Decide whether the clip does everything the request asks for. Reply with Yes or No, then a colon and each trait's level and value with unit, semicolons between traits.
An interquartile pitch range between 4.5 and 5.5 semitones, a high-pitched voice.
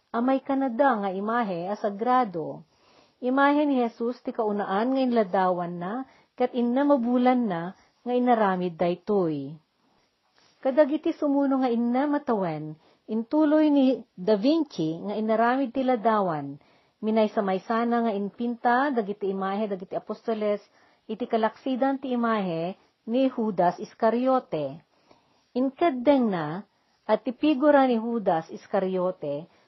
Yes: average, 5.1 semitones; high, 230 Hz